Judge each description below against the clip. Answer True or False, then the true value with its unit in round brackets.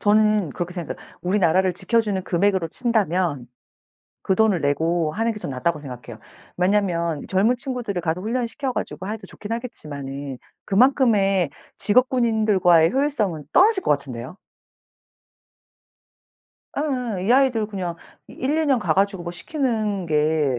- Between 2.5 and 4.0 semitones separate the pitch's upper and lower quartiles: False (5.5 semitones)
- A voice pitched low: False (195 Hz)